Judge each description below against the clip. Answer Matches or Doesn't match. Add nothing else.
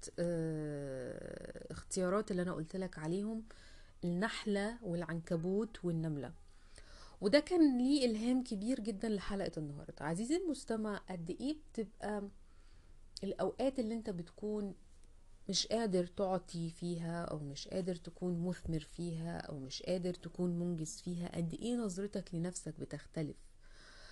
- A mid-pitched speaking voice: Matches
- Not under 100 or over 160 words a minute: Matches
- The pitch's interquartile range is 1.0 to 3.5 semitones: Doesn't match